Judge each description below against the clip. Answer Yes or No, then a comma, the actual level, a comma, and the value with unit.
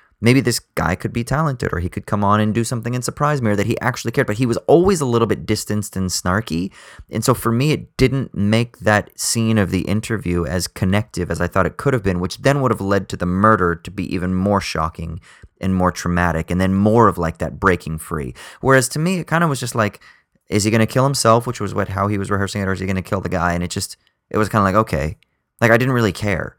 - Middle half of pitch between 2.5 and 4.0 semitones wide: No, average, 4.4 semitones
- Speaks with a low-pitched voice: Yes, low, 105 Hz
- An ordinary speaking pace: No, fast, 275 wpm